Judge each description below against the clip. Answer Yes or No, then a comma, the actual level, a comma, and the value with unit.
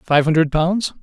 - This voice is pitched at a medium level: Yes, medium, 165 Hz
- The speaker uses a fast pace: No, average, 175 wpm